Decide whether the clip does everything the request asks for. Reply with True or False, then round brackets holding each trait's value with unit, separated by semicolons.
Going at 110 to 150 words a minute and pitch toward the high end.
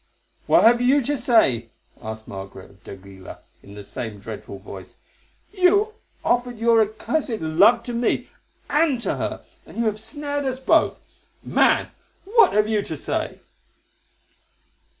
True (140 wpm; 225 Hz)